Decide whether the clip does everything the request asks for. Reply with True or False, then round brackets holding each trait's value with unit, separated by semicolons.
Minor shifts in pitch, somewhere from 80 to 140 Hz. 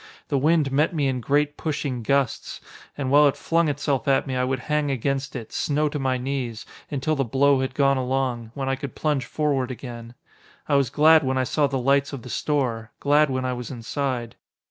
True (2.2 semitones; 135 Hz)